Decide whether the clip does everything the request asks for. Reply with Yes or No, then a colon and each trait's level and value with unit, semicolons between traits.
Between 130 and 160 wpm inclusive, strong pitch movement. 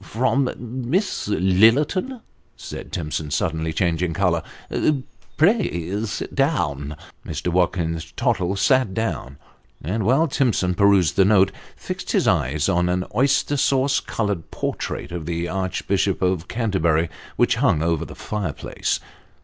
Yes: average, 140 wpm; wide, 6.4 semitones